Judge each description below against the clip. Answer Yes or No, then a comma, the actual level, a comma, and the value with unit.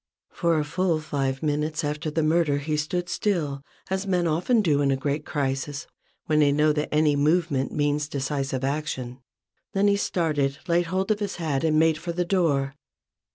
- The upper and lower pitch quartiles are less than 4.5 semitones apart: Yes, average, 3.1 semitones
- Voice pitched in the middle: Yes, medium, 150 Hz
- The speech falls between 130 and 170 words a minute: No, average, 185 wpm